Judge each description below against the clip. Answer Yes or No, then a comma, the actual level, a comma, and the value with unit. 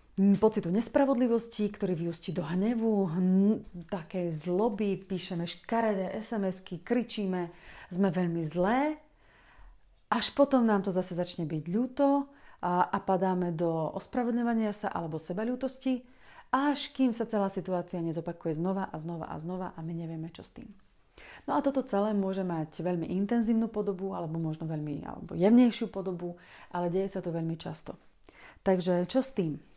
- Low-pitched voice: No, high, 190 Hz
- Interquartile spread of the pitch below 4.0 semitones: No, average, 4.4 semitones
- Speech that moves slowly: No, average, 150 wpm